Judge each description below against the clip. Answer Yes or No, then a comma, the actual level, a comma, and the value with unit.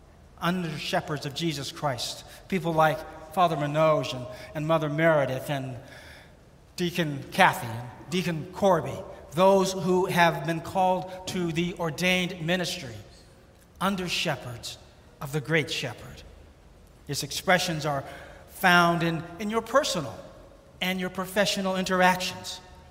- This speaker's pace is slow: Yes, slow, 120 wpm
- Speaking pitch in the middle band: Yes, medium, 165 Hz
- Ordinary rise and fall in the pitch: Yes, average, 4.4 semitones